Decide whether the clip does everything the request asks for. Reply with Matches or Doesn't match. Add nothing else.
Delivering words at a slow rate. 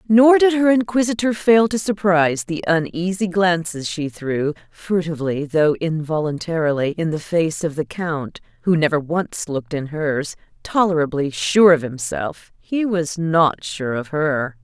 Doesn't match